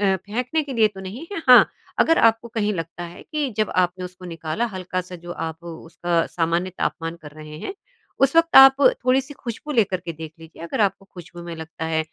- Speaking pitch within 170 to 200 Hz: Yes, medium, 185 Hz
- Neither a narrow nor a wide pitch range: No, wide, 6.2 semitones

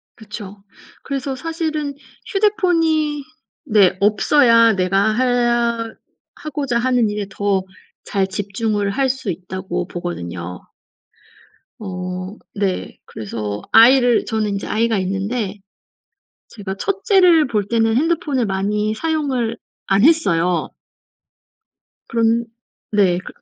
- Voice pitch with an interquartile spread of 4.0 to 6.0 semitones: Yes, average, 5.3 semitones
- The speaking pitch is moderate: No, high, 220 Hz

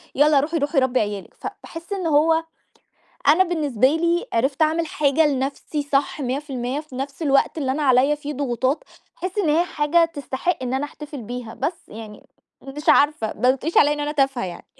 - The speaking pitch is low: No, very high, 290 Hz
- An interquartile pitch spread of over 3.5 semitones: No, average, 3.2 semitones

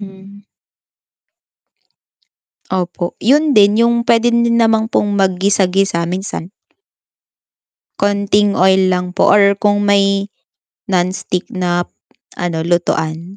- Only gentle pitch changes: Yes, narrow, 2.3 semitones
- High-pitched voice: Yes, high, 195 Hz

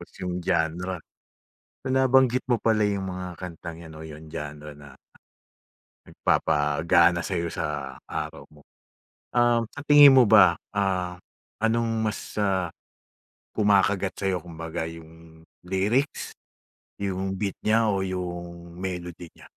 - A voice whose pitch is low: Yes, very low, 90 Hz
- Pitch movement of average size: Yes, average, 3.8 semitones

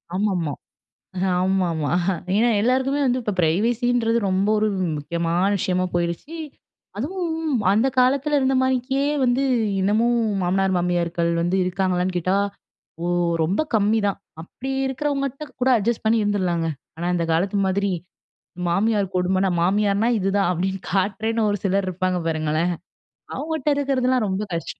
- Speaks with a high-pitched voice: Yes, high, 200 Hz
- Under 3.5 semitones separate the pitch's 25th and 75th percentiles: No, average, 5.2 semitones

